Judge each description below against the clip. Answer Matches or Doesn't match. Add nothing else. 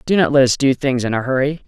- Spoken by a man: Matches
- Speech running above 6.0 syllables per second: Matches